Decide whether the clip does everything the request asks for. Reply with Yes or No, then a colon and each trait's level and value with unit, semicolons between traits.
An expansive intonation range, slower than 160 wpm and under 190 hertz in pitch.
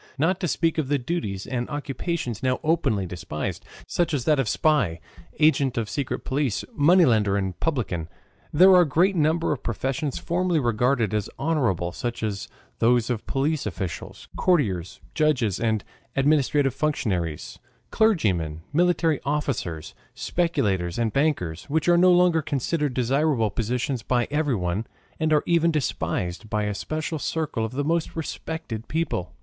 Yes: wide, 6.7 semitones; average, 150 wpm; low, 135 Hz